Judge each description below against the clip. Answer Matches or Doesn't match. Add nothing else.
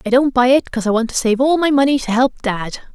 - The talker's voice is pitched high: Matches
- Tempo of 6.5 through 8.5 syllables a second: Matches